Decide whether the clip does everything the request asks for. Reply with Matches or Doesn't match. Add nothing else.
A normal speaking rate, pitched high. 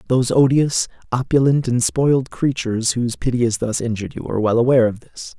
Doesn't match